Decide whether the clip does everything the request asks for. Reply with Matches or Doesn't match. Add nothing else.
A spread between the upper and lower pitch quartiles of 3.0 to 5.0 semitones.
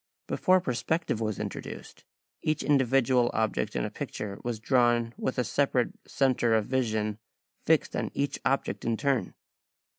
Matches